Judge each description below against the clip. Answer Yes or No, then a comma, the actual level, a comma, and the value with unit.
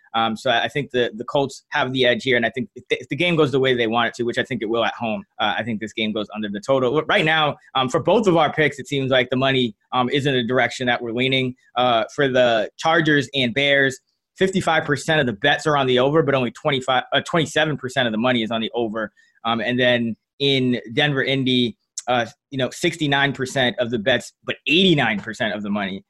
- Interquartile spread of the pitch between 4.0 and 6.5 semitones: No, average, 3.3 semitones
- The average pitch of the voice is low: Yes, low, 130 Hz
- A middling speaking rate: No, fast, 250 wpm